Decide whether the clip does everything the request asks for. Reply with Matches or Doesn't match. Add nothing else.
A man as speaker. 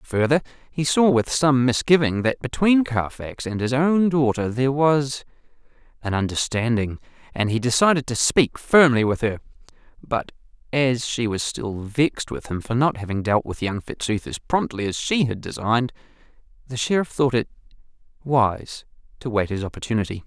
Matches